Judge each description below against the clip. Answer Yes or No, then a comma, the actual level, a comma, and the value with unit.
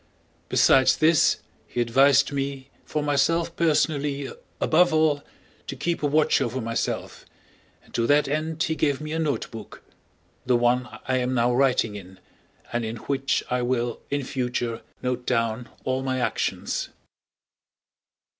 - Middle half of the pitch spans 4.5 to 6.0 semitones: No, average, 3.4 semitones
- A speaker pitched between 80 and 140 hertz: Yes, low, 135 Hz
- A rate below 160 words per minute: Yes, average, 145 wpm